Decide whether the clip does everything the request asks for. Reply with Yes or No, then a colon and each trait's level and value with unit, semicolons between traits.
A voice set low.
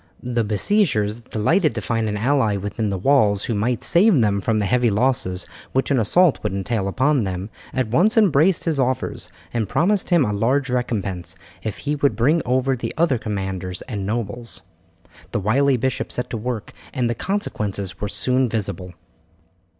Yes: low, 115 Hz